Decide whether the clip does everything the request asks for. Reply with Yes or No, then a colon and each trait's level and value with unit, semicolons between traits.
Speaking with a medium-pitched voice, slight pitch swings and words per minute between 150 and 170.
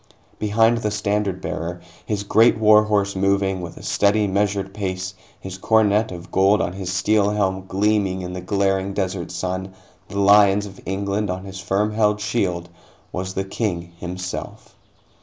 No: low, 100 Hz; narrow, 1.9 semitones; average, 160 wpm